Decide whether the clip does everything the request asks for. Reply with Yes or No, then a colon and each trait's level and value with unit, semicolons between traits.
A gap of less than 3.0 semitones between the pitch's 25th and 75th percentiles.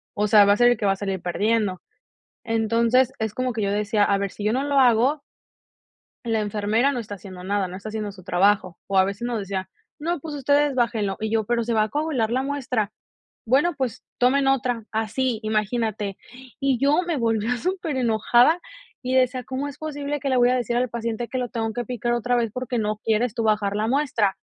No: average, 3.5 semitones